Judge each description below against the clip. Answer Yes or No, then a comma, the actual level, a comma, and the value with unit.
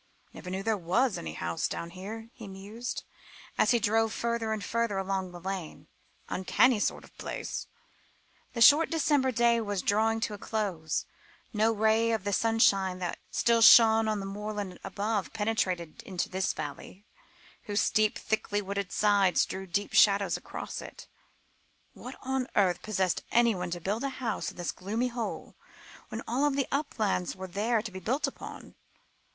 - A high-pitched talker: Yes, high, 210 Hz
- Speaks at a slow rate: No, average, 165 wpm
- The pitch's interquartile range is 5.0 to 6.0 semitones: No, average, 3.2 semitones